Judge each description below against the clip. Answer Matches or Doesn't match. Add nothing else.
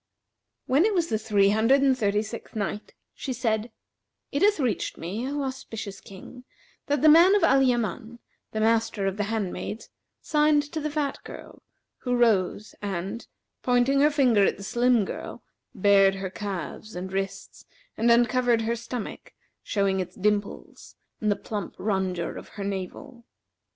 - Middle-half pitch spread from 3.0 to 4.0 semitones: Doesn't match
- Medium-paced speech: Matches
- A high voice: Matches